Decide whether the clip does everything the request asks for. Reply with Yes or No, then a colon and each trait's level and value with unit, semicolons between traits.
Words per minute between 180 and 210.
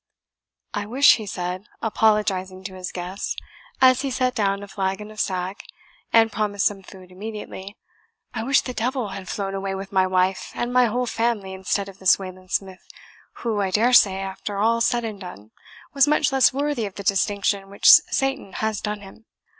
Yes: average, 185 wpm